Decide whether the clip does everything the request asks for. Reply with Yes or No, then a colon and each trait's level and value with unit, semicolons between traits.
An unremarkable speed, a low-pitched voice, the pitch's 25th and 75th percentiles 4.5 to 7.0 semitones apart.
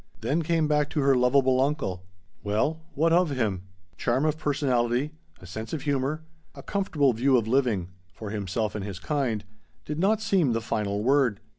Yes: average, 175 wpm; low, 130 Hz; wide, 5.4 semitones